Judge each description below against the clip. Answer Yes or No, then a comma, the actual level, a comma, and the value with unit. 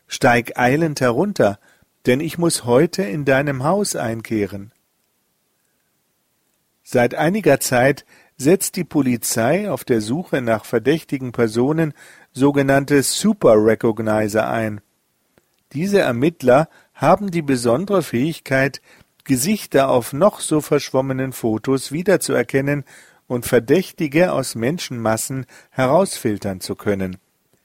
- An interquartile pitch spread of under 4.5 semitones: No, wide, 5.5 semitones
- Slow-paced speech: Yes, slow, 100 wpm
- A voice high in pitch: No, low, 135 Hz